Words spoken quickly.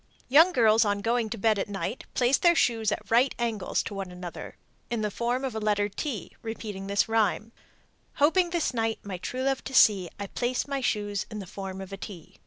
Yes: fast, 215 wpm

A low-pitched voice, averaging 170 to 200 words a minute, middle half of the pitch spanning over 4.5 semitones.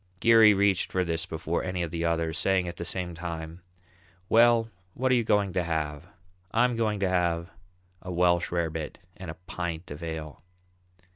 No: very low, 90 Hz; average, 180 wpm; average, 3.0 semitones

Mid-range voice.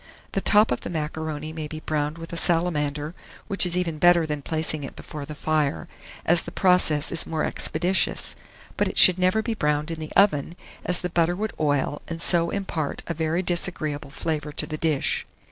Yes: medium, 160 Hz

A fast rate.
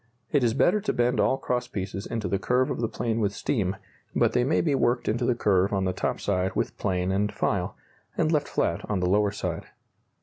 Yes: fast, 230 wpm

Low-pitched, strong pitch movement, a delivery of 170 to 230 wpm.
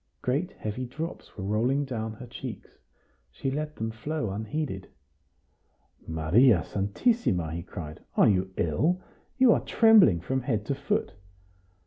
No: low, 120 Hz; wide, 7.0 semitones; slow, 135 wpm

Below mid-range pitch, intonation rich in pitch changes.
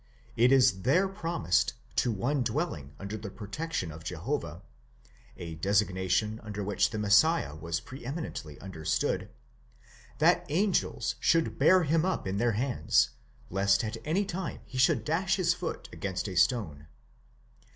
Yes: low, 110 Hz; wide, 8.7 semitones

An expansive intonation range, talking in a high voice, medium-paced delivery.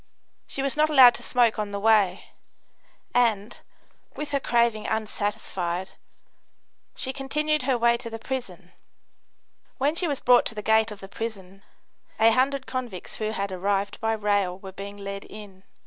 No: average, 4.1 semitones; high, 220 Hz; average, 165 wpm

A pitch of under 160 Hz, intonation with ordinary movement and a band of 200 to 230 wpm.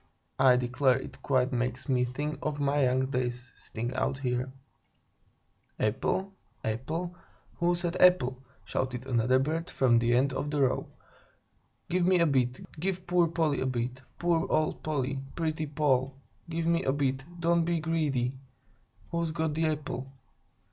No: medium, 140 Hz; average, 4.2 semitones; average, 155 wpm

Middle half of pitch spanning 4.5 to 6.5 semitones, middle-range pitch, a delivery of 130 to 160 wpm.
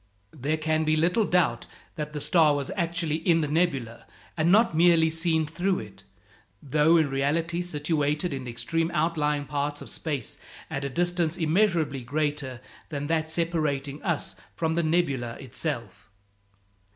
No: average, 2.8 semitones; medium, 155 Hz; average, 150 wpm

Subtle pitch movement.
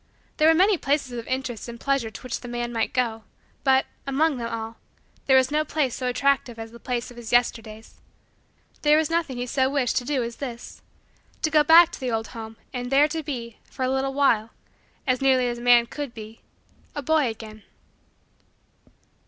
No: average, 3.1 semitones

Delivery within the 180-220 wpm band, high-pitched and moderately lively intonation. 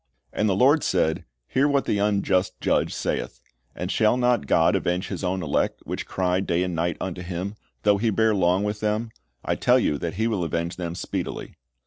No: average, 200 wpm; very low, 95 Hz; average, 3.4 semitones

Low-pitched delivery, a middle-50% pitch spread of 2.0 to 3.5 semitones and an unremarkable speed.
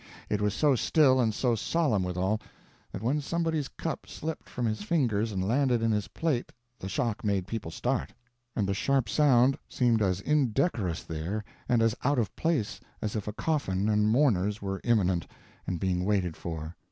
No: low, 110 Hz; wide, 5.4 semitones; average, 180 wpm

